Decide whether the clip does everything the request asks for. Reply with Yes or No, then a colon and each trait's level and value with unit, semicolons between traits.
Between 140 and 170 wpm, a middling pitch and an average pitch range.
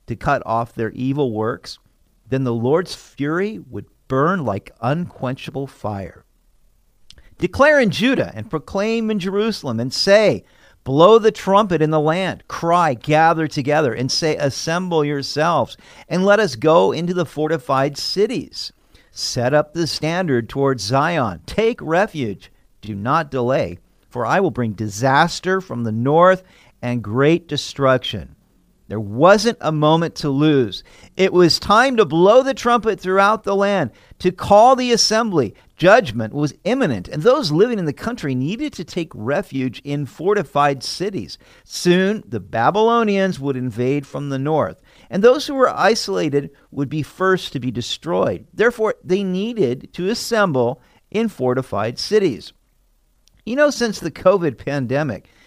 No: average, 145 wpm; medium, 155 Hz; wide, 7.1 semitones